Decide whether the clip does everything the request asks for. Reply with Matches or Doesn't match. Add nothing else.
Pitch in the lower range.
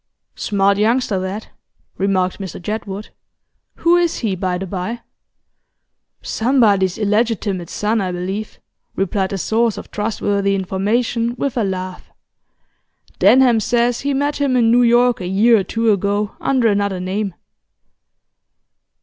Doesn't match